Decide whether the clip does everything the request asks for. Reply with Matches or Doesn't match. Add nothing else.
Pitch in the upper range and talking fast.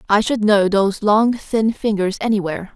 Doesn't match